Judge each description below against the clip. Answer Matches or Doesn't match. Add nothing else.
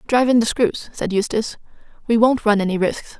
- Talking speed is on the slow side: Doesn't match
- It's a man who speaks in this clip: Doesn't match